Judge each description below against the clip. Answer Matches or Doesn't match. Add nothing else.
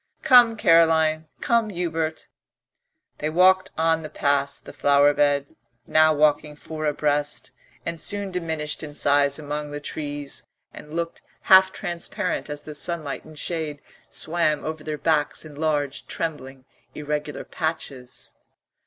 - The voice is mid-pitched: Matches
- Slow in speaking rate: Matches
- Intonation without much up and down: Matches